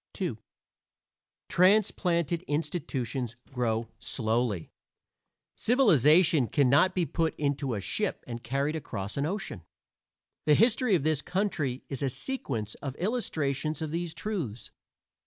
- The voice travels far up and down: Yes, wide, 6.1 semitones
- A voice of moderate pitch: Yes, medium, 150 Hz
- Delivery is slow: Yes, slow, 120 wpm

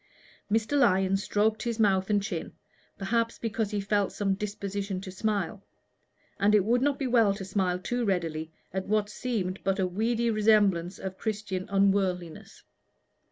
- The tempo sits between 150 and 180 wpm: Yes, average, 160 wpm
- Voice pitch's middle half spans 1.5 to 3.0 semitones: Yes, narrow, 2.4 semitones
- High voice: Yes, high, 200 Hz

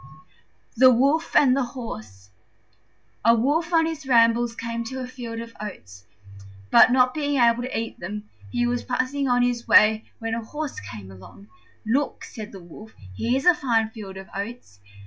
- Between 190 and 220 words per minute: No, average, 175 wpm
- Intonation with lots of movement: No, average, 3.3 semitones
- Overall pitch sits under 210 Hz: No, high, 235 Hz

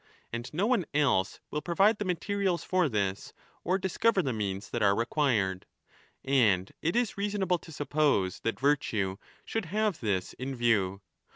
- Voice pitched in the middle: Yes, medium, 145 Hz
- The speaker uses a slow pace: No, average, 165 wpm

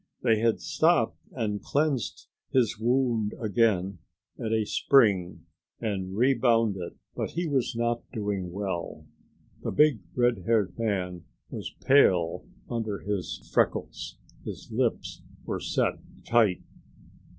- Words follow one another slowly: Yes, slow, 115 wpm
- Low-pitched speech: Yes, low, 110 Hz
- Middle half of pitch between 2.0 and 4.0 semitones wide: Yes, average, 3.7 semitones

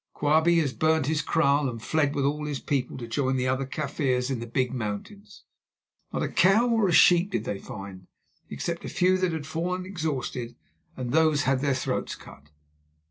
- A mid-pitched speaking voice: Yes, medium, 145 Hz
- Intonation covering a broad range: No, average, 4.2 semitones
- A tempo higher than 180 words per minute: Yes, average, 190 wpm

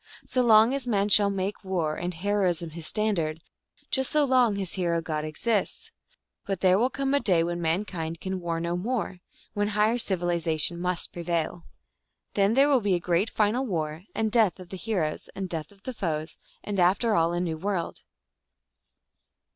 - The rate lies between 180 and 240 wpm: Yes, average, 185 wpm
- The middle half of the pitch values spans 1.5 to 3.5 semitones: No, average, 4.0 semitones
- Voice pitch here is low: No, medium, 185 Hz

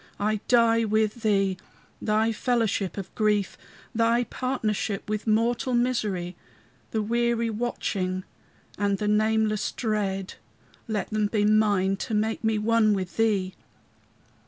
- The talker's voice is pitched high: Yes, high, 215 Hz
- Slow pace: Yes, slow, 125 wpm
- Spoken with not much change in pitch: Yes, narrow, 2.0 semitones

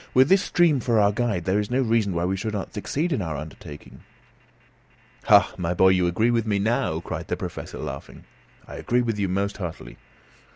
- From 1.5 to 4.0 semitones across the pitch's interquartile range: No, average, 4.5 semitones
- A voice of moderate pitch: No, low, 105 Hz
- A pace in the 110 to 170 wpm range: No, fast, 205 wpm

